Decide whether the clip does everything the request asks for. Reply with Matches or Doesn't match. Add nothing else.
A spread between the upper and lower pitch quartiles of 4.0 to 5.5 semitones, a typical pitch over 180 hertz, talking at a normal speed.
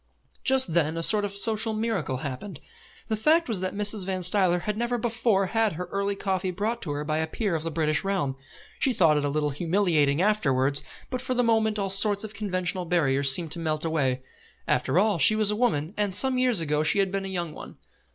Doesn't match